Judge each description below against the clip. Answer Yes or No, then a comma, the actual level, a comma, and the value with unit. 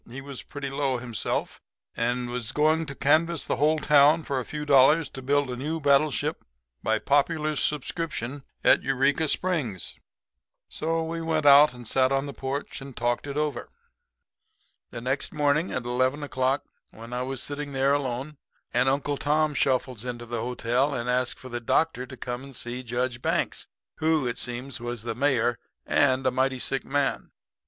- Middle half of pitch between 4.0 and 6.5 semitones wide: No, average, 2.8 semitones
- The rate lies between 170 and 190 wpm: Yes, average, 180 wpm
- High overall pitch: No, low, 135 Hz